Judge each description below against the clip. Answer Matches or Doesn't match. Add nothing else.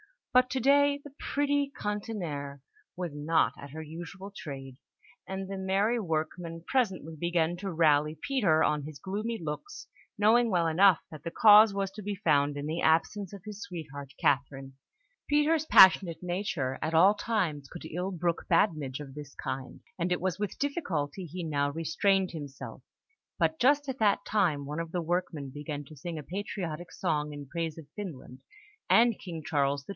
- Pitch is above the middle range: Doesn't match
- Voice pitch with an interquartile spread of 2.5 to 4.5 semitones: Doesn't match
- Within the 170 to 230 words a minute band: Matches